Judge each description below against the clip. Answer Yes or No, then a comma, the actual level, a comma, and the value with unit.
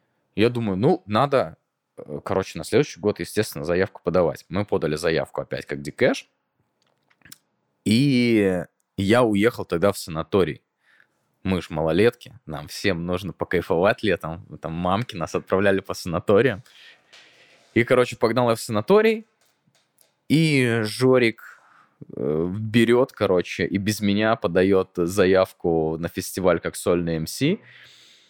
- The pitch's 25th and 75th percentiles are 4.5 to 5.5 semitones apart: Yes, average, 5.0 semitones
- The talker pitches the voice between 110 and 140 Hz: No, low, 100 Hz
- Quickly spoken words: No, average, 120 wpm